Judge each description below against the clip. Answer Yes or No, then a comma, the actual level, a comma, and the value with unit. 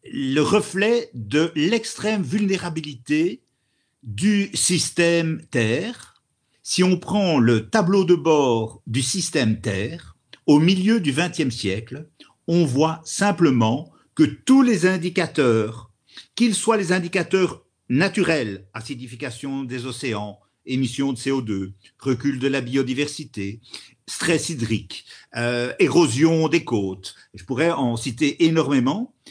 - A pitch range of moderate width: No, wide, 6.5 semitones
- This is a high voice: No, medium, 150 Hz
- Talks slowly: Yes, slow, 115 wpm